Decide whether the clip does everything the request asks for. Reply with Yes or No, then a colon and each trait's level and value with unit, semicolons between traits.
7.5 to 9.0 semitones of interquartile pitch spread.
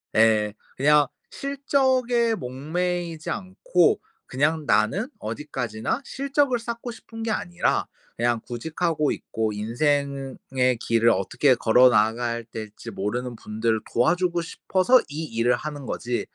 Yes: wide, 8.0 semitones